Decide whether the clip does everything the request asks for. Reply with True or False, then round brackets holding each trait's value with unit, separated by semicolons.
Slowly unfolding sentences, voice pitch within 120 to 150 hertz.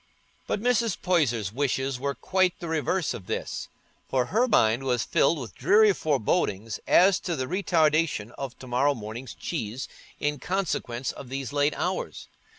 False (155 wpm; 140 Hz)